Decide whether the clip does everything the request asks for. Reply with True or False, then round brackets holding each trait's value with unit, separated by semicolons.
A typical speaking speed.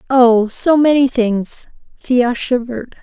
False (100 wpm)